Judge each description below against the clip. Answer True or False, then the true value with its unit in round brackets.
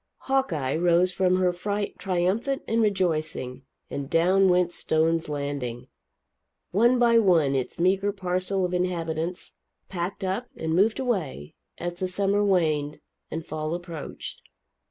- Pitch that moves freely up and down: False (3.5 semitones)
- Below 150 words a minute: True (135 wpm)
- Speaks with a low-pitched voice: False (180 Hz)